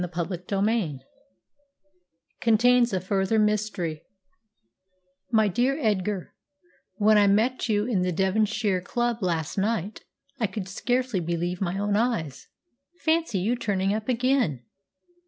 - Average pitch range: Yes, average, 3.9 semitones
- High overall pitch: Yes, high, 205 Hz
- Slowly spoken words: Yes, slow, 120 wpm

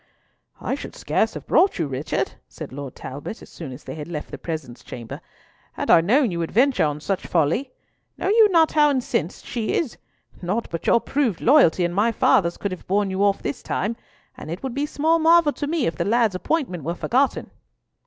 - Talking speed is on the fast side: Yes, fast, 215 wpm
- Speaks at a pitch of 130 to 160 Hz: No, high, 200 Hz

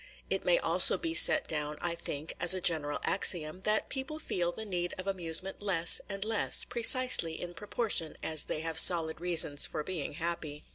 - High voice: No, medium, 175 Hz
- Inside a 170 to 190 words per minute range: Yes, average, 185 wpm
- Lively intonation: No, average, 4.1 semitones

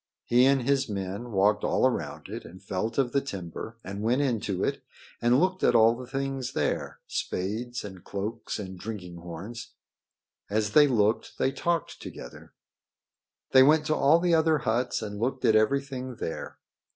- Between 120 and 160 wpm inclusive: No, average, 170 wpm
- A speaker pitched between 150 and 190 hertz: No, low, 115 Hz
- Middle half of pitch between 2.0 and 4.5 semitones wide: No, average, 5.0 semitones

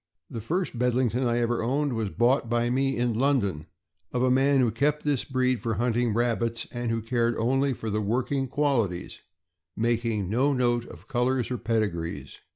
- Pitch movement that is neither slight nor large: No, narrow, 2.3 semitones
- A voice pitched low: Yes, low, 120 Hz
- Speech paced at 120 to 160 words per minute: No, average, 170 wpm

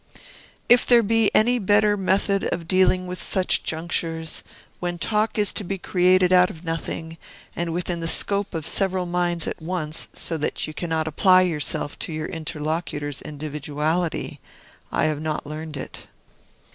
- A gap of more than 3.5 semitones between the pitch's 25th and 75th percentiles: No, average, 2.8 semitones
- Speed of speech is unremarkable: Yes, average, 160 wpm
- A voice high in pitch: No, medium, 175 Hz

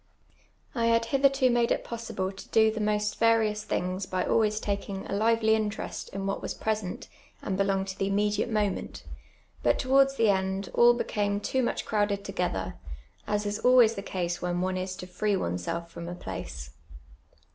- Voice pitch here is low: No, high, 205 Hz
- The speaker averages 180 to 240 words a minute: Yes, average, 185 wpm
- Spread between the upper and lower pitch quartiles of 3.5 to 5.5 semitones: No, average, 3.0 semitones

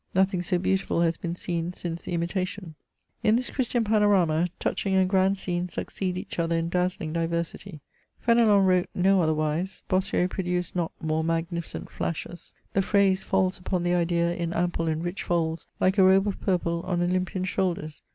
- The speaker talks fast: No, average, 170 wpm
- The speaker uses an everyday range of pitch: No, narrow, 2.1 semitones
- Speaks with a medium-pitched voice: Yes, medium, 180 Hz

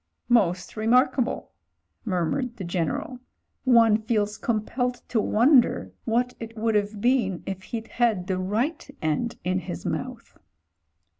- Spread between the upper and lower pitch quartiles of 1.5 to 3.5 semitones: No, average, 4.1 semitones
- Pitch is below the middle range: No, high, 220 Hz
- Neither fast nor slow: No, slow, 130 wpm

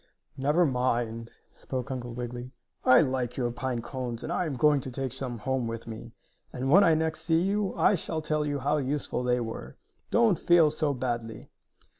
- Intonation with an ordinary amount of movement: Yes, average, 4.0 semitones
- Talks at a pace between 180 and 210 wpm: Yes, average, 190 wpm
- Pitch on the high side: No, low, 130 Hz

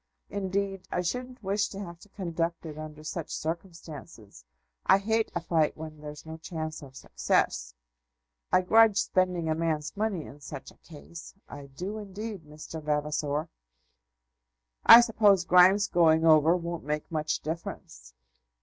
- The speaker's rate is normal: Yes, average, 150 wpm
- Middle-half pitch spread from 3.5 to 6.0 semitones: Yes, average, 4.1 semitones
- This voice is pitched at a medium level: Yes, medium, 165 Hz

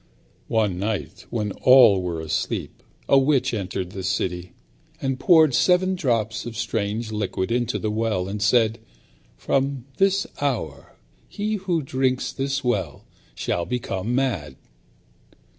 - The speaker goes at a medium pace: No, slow, 130 wpm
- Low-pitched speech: Yes, low, 115 Hz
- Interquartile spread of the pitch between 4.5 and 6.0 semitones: Yes, wide, 5.5 semitones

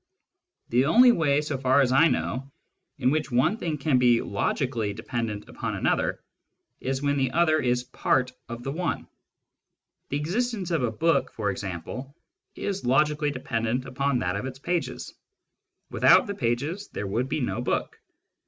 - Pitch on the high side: No, low, 135 Hz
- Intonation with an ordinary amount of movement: Yes, average, 4.2 semitones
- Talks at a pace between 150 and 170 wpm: Yes, average, 160 wpm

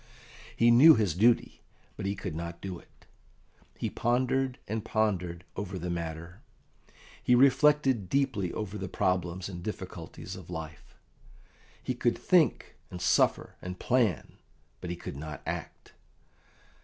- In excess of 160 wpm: No, average, 140 wpm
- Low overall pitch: Yes, very low, 95 Hz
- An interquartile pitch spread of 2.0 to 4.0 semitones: No, average, 5.3 semitones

